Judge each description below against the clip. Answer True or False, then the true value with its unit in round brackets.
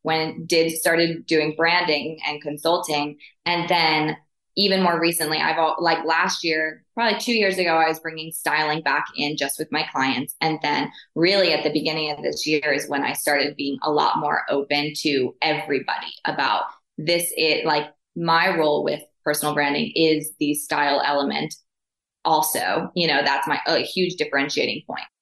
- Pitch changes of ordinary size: False (1.9 semitones)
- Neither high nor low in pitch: True (155 Hz)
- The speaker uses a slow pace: False (175 wpm)